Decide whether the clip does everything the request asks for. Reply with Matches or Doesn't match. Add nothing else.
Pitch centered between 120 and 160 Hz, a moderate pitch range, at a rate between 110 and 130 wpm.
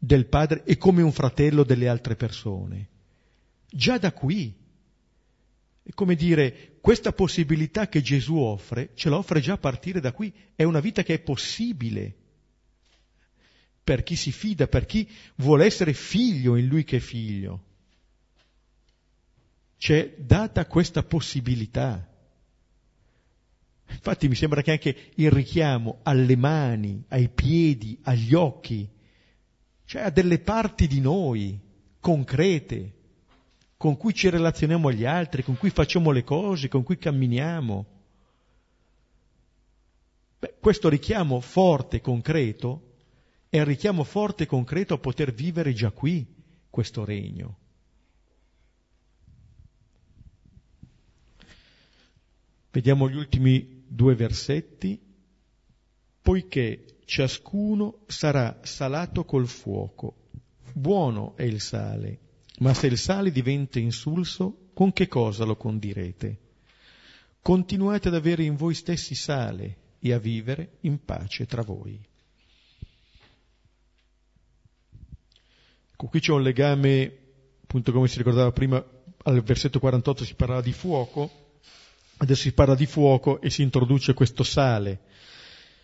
Doesn't match